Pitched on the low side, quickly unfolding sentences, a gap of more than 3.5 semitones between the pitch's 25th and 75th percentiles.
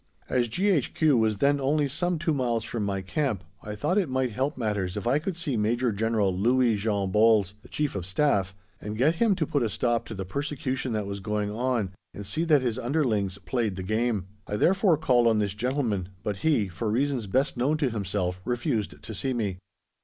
Yes: low, 115 Hz; fast, 210 wpm; average, 5.3 semitones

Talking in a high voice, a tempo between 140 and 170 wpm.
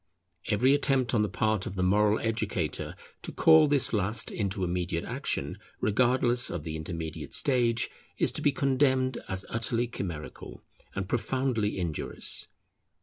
No: low, 110 Hz; average, 145 wpm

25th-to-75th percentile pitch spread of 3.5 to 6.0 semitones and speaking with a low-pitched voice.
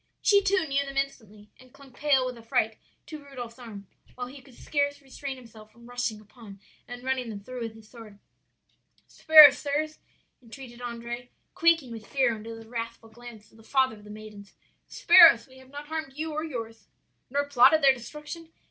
No: average, 3.8 semitones; very high, 250 Hz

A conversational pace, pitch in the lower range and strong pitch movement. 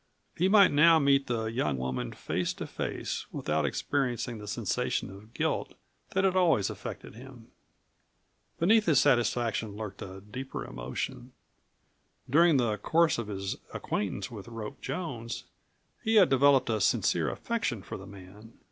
Yes: average, 150 wpm; low, 120 Hz; wide, 6.1 semitones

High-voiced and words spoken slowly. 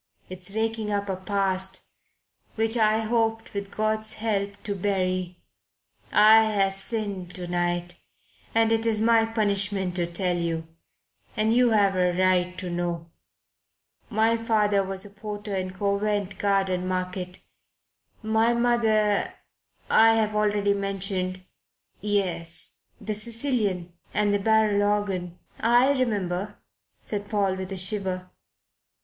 Yes: high, 200 Hz; slow, 130 wpm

